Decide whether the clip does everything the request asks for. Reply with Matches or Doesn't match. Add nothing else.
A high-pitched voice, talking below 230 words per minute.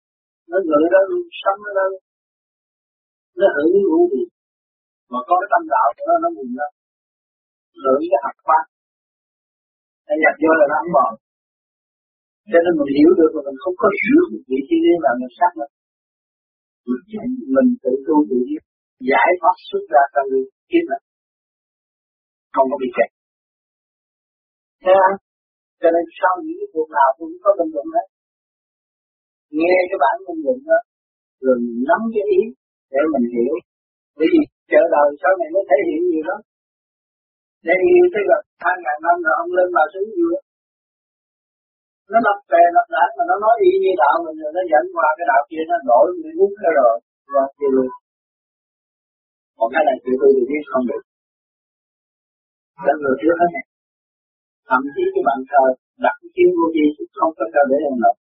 Matches